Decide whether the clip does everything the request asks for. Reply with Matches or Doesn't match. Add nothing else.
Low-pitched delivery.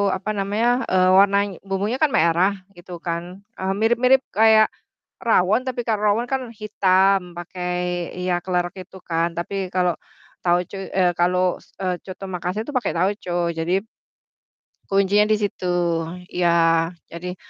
Doesn't match